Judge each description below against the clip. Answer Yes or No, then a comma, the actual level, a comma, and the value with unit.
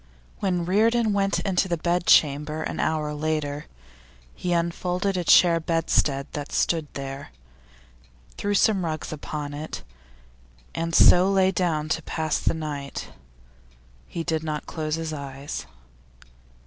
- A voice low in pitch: No, medium, 160 Hz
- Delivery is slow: Yes, slow, 130 wpm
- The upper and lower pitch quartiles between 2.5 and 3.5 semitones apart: Yes, average, 3.0 semitones